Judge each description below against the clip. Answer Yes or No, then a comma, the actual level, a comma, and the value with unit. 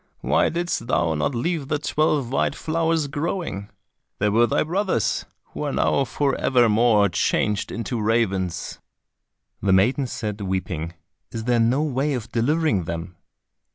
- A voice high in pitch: No, low, 120 Hz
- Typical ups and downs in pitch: No, wide, 6.5 semitones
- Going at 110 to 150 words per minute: Yes, average, 145 wpm